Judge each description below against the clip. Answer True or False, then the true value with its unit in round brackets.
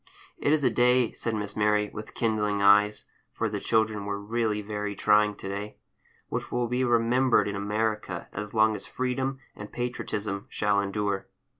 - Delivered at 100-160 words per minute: False (170 wpm)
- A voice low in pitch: True (105 Hz)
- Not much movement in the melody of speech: True (2.3 semitones)